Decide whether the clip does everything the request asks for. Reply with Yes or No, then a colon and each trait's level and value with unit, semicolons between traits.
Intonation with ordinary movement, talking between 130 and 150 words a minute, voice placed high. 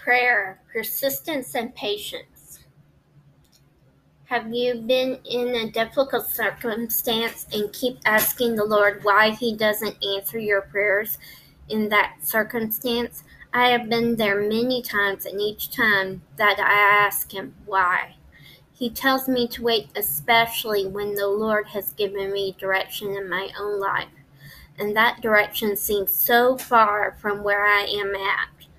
Yes: average, 3.0 semitones; average, 140 wpm; high, 210 Hz